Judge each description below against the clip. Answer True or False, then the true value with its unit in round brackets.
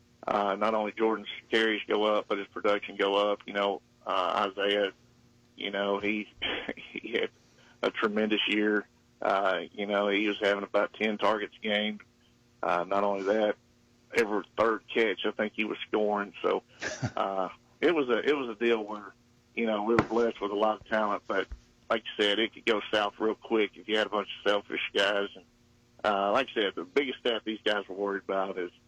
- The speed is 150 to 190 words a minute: False (205 wpm)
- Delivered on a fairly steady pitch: True (1.6 semitones)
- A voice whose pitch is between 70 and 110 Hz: True (105 Hz)